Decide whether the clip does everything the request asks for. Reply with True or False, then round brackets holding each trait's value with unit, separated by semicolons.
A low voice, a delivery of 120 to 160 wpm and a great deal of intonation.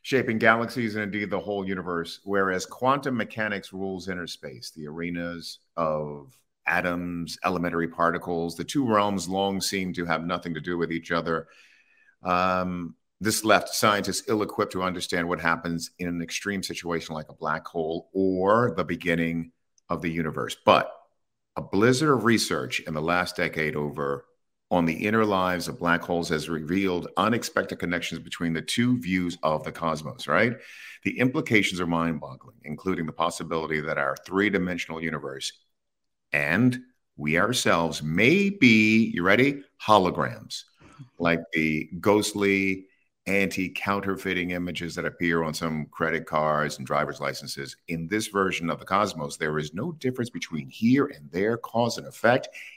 False (90 Hz; 155 wpm; 3.0 semitones)